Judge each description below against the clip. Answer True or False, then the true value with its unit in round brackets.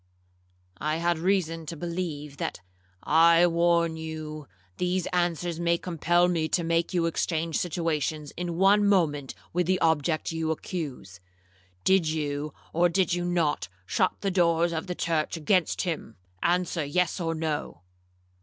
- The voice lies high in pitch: False (165 Hz)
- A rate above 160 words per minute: False (145 wpm)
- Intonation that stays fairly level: True (2.1 semitones)